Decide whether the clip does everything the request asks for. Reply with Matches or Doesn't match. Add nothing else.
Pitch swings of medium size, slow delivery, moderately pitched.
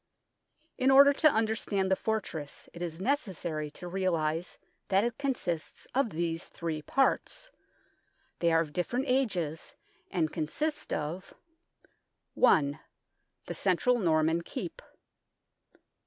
Doesn't match